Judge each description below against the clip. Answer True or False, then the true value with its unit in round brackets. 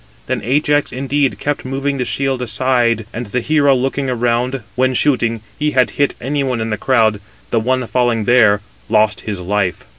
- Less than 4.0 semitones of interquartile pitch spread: True (3.0 semitones)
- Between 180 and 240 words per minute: True (185 wpm)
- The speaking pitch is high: False (125 Hz)